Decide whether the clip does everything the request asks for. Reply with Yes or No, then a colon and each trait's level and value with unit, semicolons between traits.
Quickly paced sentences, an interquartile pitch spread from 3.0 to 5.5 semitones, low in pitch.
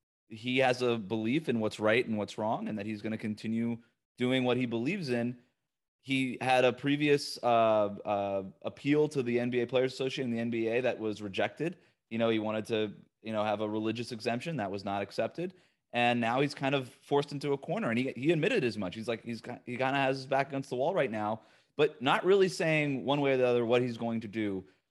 Yes: fast, 235 wpm; average, 3.6 semitones; low, 120 Hz